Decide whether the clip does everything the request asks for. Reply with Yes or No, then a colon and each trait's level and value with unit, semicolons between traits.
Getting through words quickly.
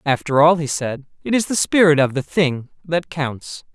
Yes: fast, 210 wpm